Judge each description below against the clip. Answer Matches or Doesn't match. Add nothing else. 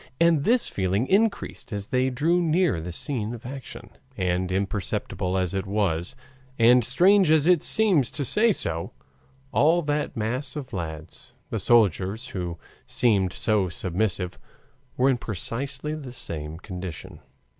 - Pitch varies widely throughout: Matches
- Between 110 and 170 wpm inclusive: Matches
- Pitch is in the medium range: Doesn't match